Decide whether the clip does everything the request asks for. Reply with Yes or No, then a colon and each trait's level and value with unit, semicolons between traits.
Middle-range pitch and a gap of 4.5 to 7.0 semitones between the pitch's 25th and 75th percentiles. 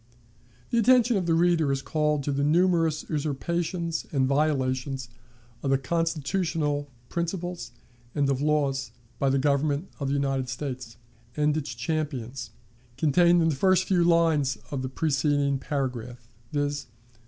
No: medium, 145 Hz; average, 3.3 semitones